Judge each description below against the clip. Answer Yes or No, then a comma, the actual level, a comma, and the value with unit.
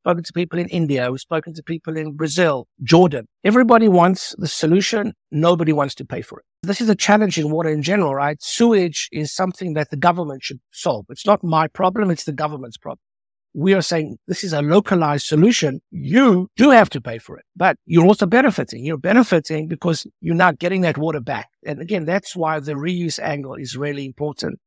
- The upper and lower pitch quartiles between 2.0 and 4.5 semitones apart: Yes, average, 3.7 semitones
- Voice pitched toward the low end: No, medium, 165 Hz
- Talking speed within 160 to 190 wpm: No, fast, 205 wpm